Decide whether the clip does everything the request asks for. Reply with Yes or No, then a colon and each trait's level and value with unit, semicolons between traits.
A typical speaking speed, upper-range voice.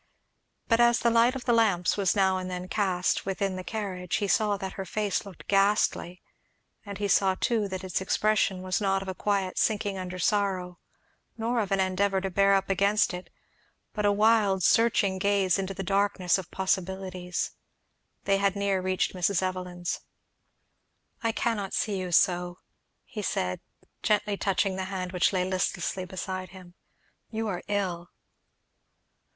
Yes: average, 165 wpm; high, 195 Hz